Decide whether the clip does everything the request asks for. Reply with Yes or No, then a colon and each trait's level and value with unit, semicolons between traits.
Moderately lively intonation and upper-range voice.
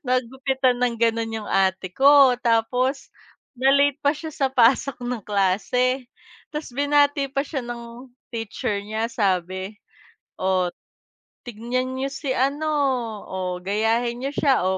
Yes: average, 3.8 semitones; high, 245 Hz